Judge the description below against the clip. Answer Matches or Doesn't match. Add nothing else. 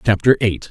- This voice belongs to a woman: Doesn't match